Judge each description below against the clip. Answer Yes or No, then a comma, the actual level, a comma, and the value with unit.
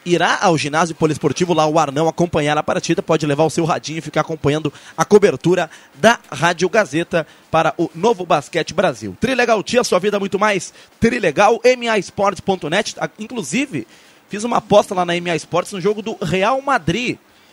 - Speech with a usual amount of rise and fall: Yes, average, 4.6 semitones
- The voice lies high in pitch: No, medium, 175 Hz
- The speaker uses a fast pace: No, average, 170 wpm